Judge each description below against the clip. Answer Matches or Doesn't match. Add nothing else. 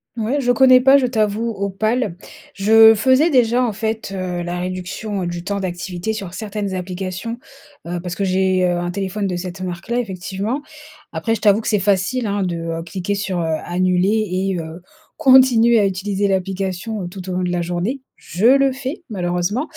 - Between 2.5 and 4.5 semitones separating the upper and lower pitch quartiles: Matches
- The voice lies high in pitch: Matches